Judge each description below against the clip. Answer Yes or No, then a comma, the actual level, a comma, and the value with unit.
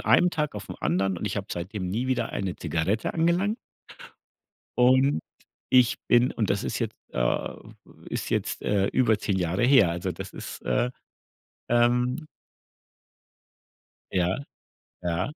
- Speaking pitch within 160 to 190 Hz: No, low, 110 Hz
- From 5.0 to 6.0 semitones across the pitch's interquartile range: Yes, wide, 5.6 semitones